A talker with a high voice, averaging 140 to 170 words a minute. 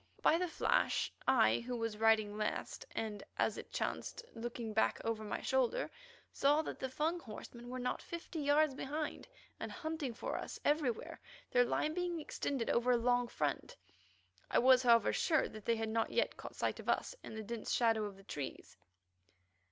No: high, 245 Hz; average, 185 wpm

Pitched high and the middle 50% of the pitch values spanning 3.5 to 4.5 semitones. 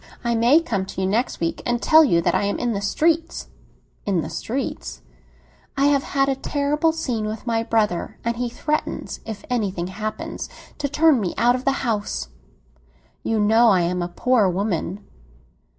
No: high, 225 Hz; average, 5.3 semitones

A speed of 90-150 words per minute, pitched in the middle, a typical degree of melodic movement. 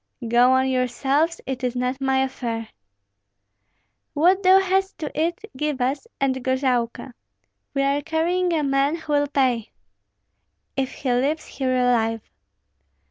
No: slow, 135 wpm; very high, 270 Hz; average, 3.4 semitones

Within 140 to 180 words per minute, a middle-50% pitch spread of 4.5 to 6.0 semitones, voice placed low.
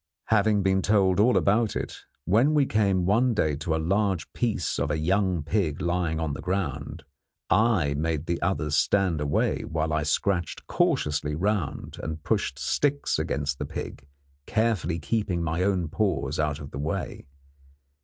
Yes: average, 165 wpm; average, 4.9 semitones; very low, 85 Hz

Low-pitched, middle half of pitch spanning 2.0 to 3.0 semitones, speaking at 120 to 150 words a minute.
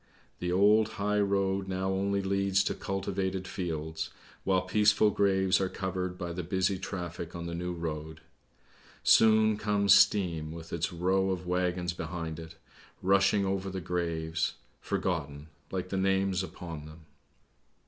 Yes: very low, 95 Hz; narrow, 2.4 semitones; average, 145 wpm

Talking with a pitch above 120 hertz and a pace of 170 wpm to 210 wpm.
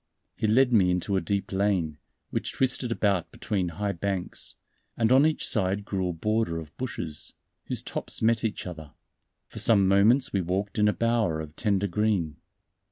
No: low, 100 Hz; average, 175 wpm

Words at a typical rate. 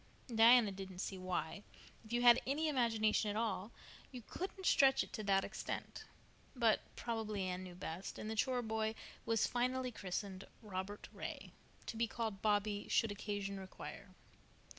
Yes: average, 160 wpm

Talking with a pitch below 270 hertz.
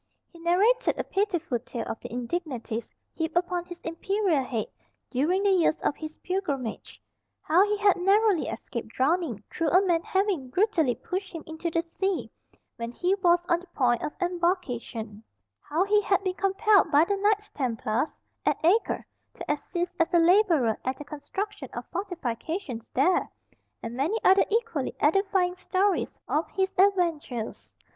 No: very high, 345 Hz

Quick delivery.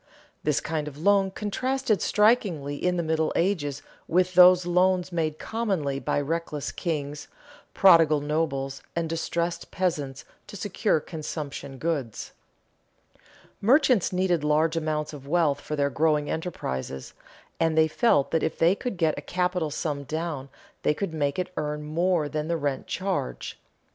No: average, 150 wpm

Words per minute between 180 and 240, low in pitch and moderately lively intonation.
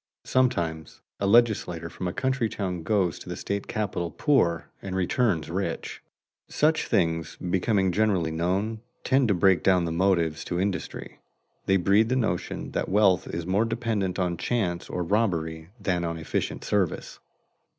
No: average, 155 wpm; very low, 95 Hz; average, 4.0 semitones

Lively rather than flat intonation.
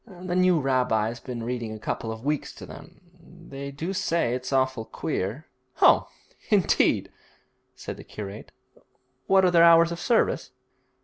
Yes: wide, 6.4 semitones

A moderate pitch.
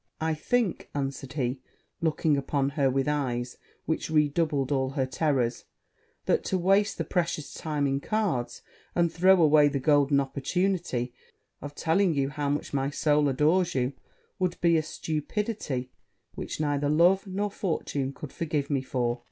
Yes: medium, 145 Hz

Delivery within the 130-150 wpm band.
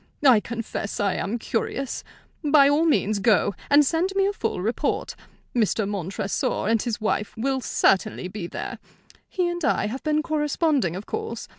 No: average, 165 wpm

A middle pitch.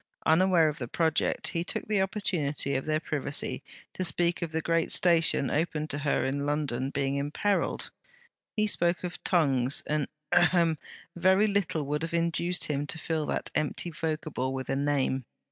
Yes: medium, 155 Hz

